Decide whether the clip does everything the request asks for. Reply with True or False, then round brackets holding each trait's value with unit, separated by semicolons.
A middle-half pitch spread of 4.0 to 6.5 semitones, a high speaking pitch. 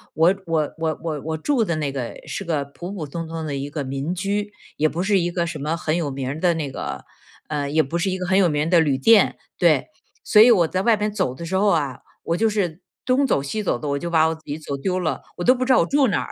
False (4.5 semitones; 165 Hz)